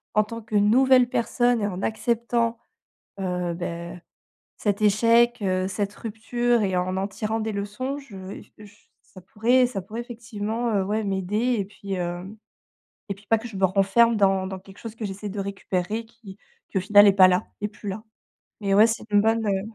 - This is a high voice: Yes, high, 210 Hz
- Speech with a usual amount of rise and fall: Yes, average, 3.0 semitones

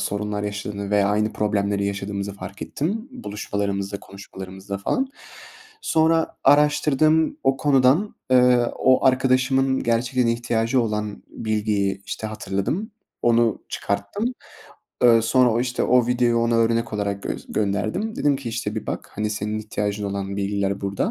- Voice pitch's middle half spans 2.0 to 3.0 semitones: No, average, 4.2 semitones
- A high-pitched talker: No, low, 110 Hz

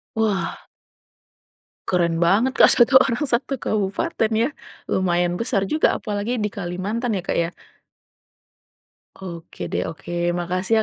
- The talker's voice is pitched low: No, high, 200 Hz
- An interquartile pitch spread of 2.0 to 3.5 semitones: No, average, 4.8 semitones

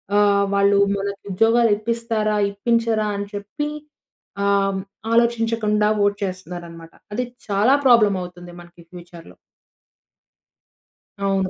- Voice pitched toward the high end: Yes, high, 200 Hz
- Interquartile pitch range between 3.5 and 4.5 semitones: No, average, 2.9 semitones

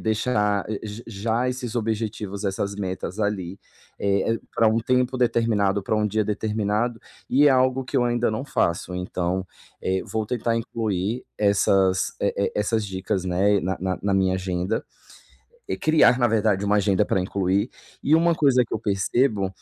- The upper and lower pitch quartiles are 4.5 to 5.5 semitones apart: No, average, 3.3 semitones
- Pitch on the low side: Yes, low, 105 Hz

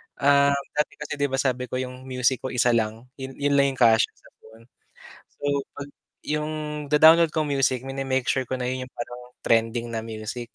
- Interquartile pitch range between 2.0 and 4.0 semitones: Yes, average, 2.9 semitones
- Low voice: Yes, low, 130 Hz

